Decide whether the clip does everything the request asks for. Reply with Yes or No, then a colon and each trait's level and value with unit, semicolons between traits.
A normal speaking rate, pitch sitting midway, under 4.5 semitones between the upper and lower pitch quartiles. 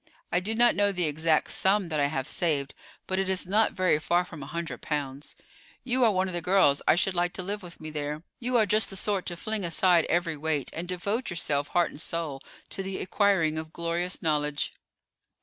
No: fast, 220 wpm; medium, 175 Hz; average, 3.7 semitones